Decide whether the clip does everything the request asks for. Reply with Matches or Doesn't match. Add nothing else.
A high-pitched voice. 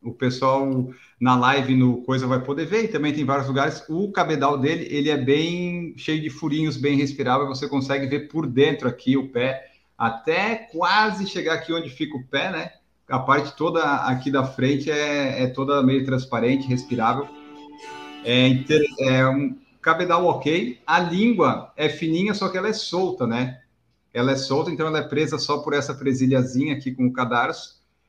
Doesn't match